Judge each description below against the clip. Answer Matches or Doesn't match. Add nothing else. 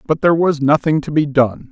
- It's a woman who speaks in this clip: Doesn't match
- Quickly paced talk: Matches